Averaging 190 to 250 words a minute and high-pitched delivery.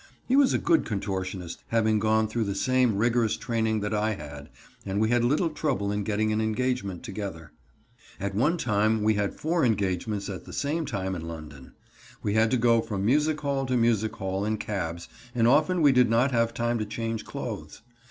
No: average, 200 wpm; low, 110 Hz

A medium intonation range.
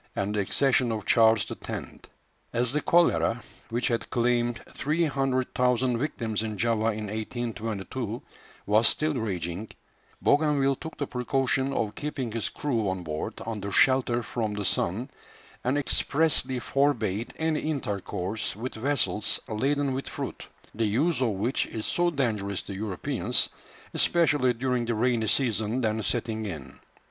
Yes: average, 3.9 semitones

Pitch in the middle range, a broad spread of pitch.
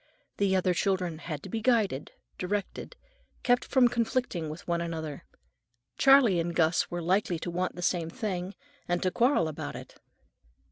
No: medium, 180 Hz; average, 4.1 semitones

